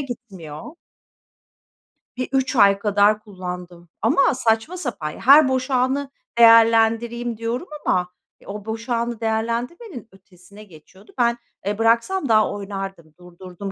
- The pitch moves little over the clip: No, average, 3.8 semitones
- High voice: Yes, high, 225 Hz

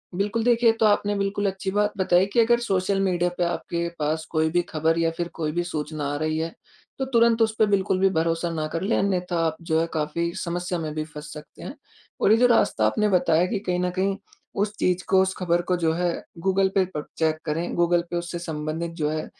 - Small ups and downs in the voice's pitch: No, average, 3.3 semitones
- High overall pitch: No, medium, 175 Hz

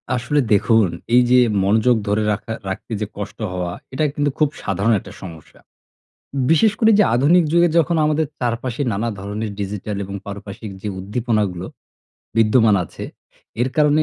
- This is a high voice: No, low, 115 Hz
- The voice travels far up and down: Yes, wide, 6.2 semitones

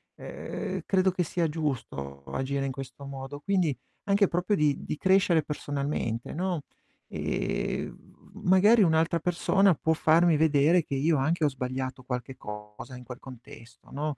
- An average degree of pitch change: Yes, average, 4.7 semitones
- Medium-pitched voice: Yes, medium, 150 Hz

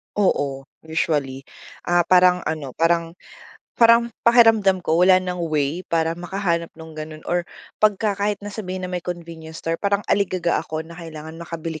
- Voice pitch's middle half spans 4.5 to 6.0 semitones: No, average, 2.9 semitones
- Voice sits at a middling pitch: Yes, medium, 170 Hz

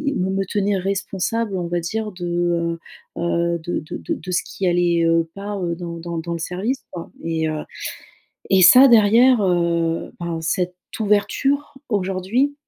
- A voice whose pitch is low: No, medium, 180 Hz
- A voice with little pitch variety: No, average, 3.2 semitones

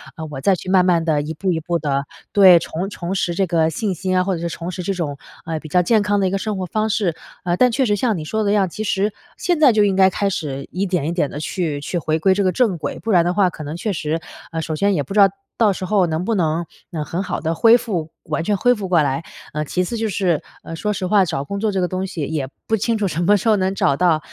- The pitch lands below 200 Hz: Yes, medium, 185 Hz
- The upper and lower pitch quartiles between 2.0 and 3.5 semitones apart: No, average, 3.9 semitones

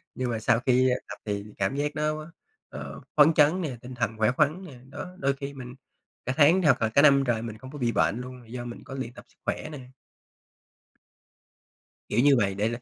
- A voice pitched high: No, low, 130 Hz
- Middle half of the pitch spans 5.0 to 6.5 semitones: No, average, 3.8 semitones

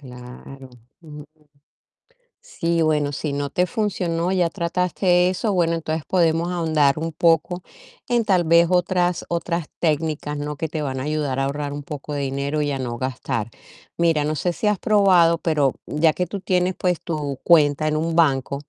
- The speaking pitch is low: No, medium, 160 Hz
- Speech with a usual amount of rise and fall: Yes, average, 3.3 semitones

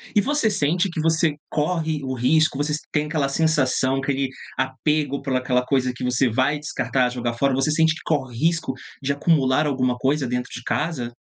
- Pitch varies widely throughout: No, average, 3.3 semitones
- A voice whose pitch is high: No, medium, 140 Hz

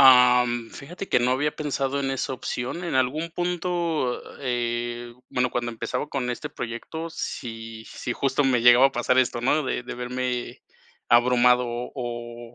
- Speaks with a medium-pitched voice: No, low, 125 Hz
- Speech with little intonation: Yes, narrow, 2.3 semitones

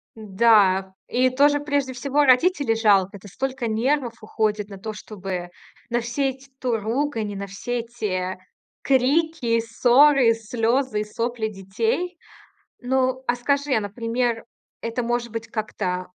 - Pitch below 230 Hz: No, high, 235 Hz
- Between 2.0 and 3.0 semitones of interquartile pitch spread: No, average, 3.6 semitones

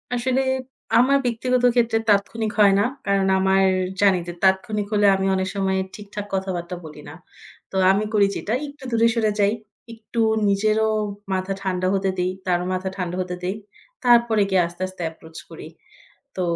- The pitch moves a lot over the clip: No, average, 2.9 semitones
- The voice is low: No, high, 200 Hz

